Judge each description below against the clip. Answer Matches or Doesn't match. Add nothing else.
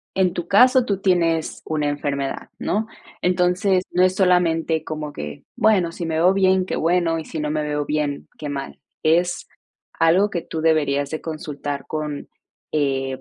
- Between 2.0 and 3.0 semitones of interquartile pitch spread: Doesn't match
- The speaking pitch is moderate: Matches